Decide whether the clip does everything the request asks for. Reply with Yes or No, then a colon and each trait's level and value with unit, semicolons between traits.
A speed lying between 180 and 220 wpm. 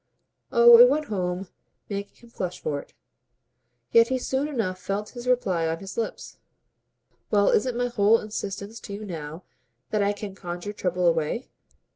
No: average, 165 wpm